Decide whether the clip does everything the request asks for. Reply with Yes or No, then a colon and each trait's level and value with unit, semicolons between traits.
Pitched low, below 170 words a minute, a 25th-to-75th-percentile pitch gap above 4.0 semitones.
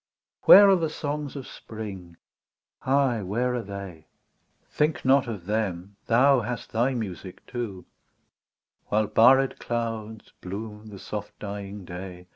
Yes: low, 110 Hz; average, 140 wpm; average, 4.4 semitones